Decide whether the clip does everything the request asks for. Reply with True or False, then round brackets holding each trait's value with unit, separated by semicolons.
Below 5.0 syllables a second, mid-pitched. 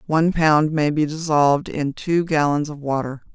True (4.8 syllables/s; 150 Hz)